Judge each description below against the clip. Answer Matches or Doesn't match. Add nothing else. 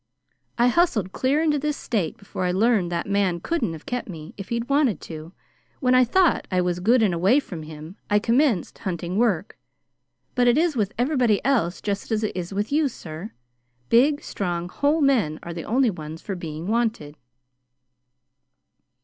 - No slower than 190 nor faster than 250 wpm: Doesn't match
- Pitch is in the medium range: Doesn't match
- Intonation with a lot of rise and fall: Matches